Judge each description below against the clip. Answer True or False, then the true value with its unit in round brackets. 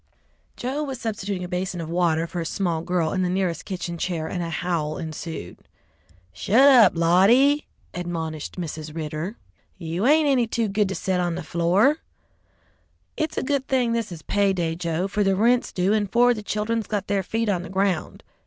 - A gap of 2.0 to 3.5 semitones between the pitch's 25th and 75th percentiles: False (4.8 semitones)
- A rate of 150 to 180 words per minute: False (195 wpm)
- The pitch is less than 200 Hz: True (185 Hz)